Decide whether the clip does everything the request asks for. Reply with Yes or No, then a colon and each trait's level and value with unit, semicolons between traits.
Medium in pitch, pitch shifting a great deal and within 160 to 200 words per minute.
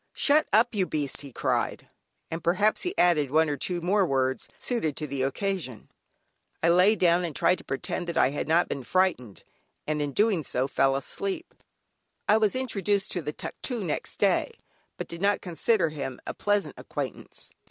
Yes: medium, 170 Hz; wide, 5.9 semitones; average, 185 wpm